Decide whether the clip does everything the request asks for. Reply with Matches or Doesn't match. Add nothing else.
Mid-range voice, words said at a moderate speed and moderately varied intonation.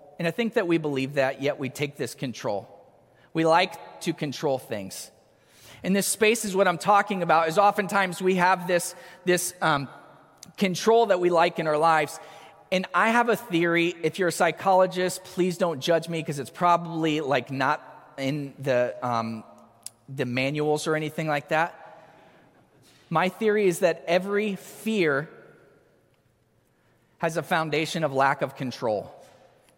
Matches